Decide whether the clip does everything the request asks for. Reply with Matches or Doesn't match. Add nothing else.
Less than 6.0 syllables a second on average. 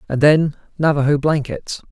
Matches